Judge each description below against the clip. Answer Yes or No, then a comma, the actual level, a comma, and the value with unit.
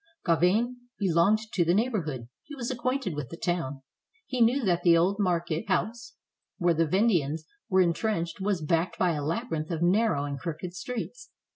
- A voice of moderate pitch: Yes, medium, 180 Hz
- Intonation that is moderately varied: Yes, average, 4.9 semitones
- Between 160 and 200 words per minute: Yes, average, 175 wpm